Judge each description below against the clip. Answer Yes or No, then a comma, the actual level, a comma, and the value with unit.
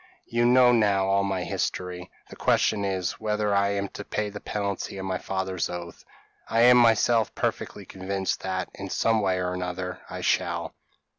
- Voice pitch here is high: No, low, 100 Hz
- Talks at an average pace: Yes, average, 175 wpm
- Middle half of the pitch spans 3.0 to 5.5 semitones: No, narrow, 2.5 semitones